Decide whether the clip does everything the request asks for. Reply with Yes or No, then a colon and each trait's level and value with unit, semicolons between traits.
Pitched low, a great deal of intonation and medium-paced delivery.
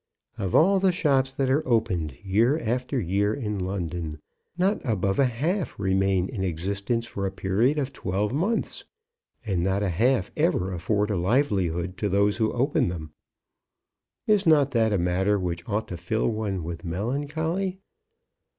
Yes: low, 105 Hz; wide, 6.3 semitones; average, 160 wpm